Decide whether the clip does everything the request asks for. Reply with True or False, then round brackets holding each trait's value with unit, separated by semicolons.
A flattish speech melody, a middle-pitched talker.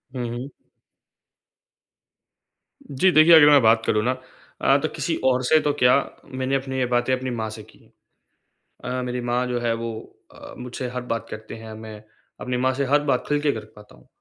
False (2.3 semitones; 125 Hz)